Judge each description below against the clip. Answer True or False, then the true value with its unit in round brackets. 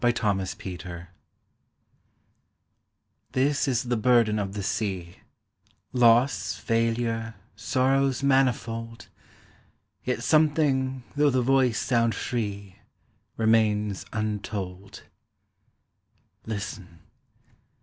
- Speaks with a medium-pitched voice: False (115 Hz)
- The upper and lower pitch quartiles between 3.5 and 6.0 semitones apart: True (4.0 semitones)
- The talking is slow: True (75 wpm)